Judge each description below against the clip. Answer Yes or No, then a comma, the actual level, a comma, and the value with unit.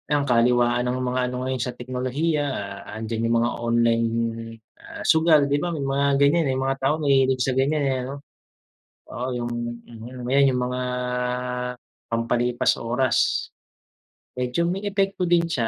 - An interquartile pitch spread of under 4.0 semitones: Yes, average, 2.7 semitones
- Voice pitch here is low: Yes, low, 130 Hz